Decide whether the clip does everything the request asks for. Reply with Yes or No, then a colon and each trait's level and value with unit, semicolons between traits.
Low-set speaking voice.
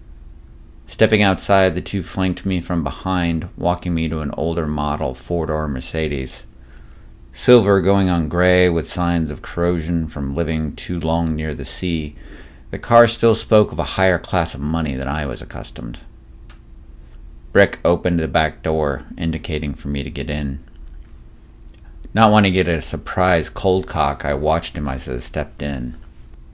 Yes: very low, 80 Hz